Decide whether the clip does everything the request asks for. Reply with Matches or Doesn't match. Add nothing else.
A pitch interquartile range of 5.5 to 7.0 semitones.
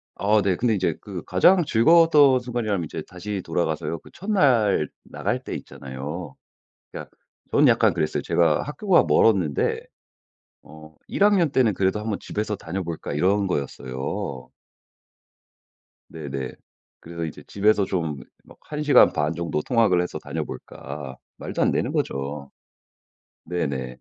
Matches